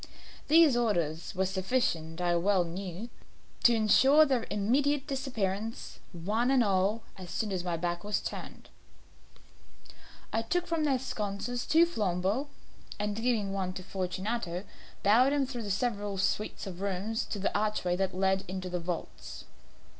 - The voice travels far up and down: No, average, 4.6 semitones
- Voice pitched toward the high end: Yes, high, 205 Hz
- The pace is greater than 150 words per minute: No, average, 145 wpm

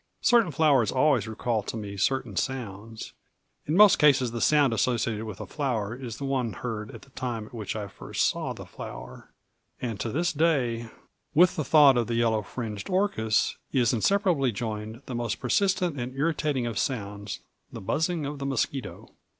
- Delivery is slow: No, average, 180 wpm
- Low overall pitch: Yes, low, 125 Hz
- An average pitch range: Yes, average, 4.6 semitones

